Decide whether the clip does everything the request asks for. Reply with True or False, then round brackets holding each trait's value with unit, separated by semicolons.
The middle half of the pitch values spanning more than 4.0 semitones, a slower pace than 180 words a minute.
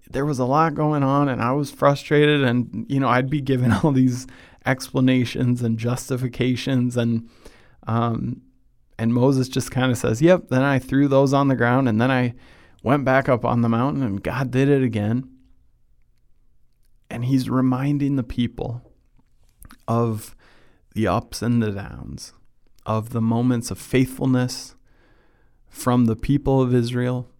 False (2.4 semitones; 160 wpm)